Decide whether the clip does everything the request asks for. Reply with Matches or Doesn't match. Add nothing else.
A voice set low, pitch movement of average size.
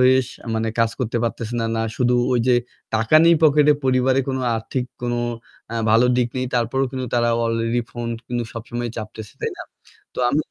Doesn't match